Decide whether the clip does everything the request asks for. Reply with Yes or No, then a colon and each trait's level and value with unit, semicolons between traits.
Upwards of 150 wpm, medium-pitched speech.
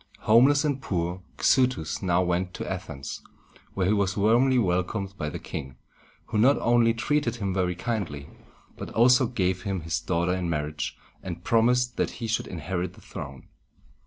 No: average, 165 wpm; very low, 95 Hz